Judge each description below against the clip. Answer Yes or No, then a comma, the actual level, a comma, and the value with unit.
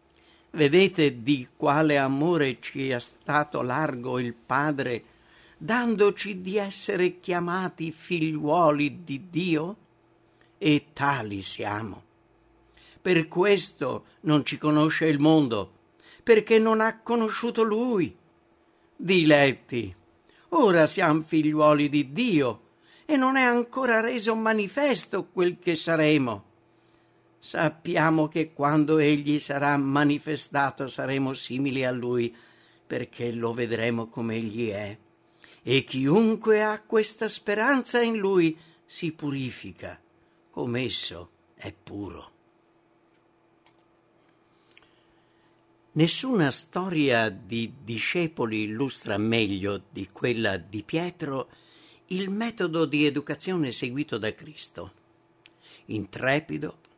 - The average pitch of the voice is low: No, medium, 150 Hz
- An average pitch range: No, wide, 6.6 semitones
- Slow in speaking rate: Yes, slow, 100 wpm